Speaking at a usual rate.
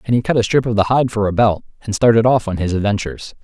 No: fast, 295 wpm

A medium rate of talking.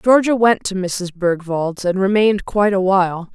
Yes: average, 180 wpm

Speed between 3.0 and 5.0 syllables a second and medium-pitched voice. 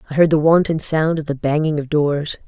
No: 5.4 syllables/s; medium, 155 Hz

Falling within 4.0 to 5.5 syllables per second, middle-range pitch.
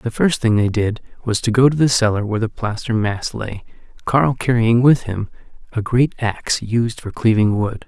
No: 4.9 syllables/s; low, 115 Hz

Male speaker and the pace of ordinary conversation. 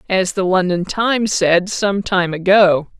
No: female; average, 160 wpm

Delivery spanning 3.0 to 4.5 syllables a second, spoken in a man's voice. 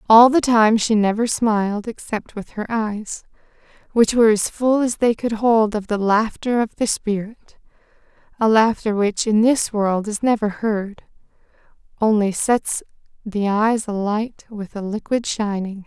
No: 4.2 syllables/s; female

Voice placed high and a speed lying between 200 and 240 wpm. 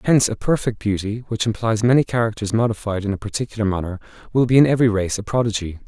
No: low, 110 Hz; fast, 205 wpm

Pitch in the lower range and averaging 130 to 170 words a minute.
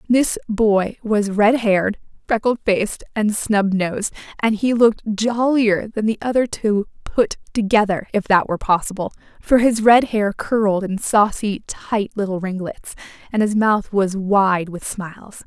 No: high, 210 Hz; average, 160 wpm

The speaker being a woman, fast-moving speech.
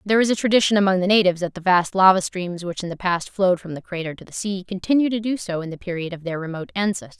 Yes: female; fast, 285 wpm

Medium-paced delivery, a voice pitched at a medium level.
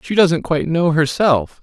Yes: average, 185 wpm; medium, 160 Hz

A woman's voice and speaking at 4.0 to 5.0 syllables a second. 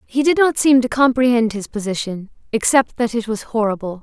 No: female; 5.4 syllables/s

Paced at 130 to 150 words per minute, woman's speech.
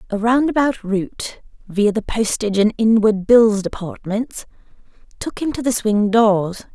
Yes: average, 140 wpm; female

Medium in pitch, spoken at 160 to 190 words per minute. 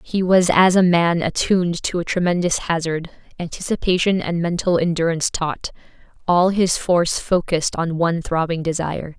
No: medium, 170 Hz; average, 150 wpm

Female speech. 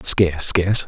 No: male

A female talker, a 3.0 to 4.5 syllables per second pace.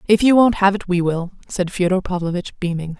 No: female; 5.7 syllables/s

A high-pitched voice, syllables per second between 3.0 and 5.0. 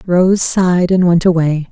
No: medium, 175 Hz; 4.5 syllables/s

